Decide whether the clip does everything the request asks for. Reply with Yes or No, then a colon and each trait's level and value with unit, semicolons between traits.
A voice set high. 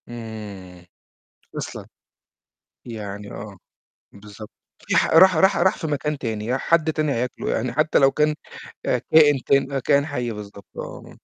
No: low, 125 Hz